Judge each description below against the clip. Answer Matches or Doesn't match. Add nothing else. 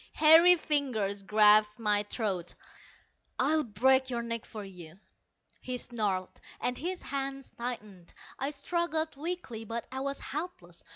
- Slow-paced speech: Matches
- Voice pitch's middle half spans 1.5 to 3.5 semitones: Doesn't match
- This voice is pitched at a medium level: Doesn't match